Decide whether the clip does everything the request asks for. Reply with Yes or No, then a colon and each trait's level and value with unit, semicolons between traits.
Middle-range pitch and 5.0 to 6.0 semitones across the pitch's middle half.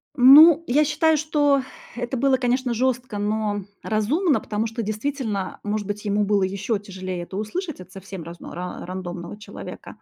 No: high, 215 Hz; average, 5.3 semitones